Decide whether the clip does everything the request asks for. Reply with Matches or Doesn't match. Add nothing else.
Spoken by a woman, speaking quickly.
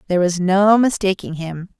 Doesn't match